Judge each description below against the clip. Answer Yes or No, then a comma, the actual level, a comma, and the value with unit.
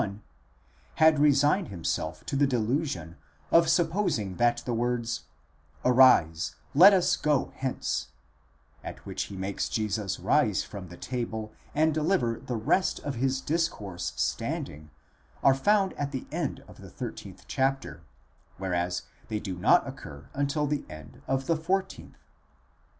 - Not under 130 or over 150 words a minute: Yes, average, 140 wpm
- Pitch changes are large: Yes, wide, 7.0 semitones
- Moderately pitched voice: No, low, 130 Hz